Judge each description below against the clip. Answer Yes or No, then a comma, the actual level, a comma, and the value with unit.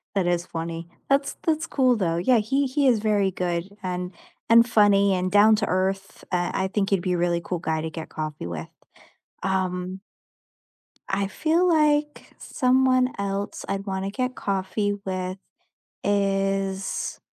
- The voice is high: Yes, high, 195 Hz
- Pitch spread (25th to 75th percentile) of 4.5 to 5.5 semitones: No, average, 3.9 semitones